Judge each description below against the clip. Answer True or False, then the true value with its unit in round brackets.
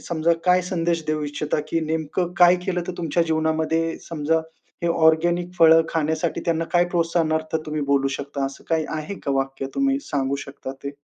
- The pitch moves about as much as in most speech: False (2.1 semitones)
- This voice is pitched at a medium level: True (160 Hz)